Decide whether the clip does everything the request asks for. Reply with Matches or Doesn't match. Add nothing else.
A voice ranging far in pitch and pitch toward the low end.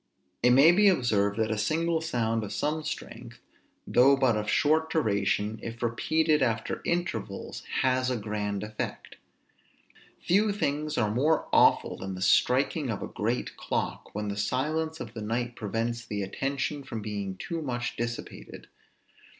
Matches